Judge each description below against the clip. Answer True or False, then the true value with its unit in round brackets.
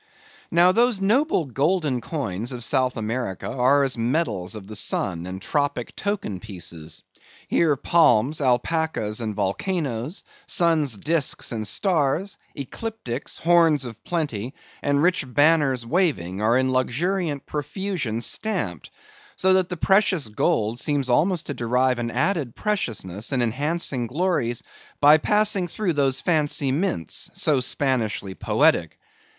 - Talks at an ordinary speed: False (130 wpm)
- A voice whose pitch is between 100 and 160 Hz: True (140 Hz)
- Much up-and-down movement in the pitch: True (6.5 semitones)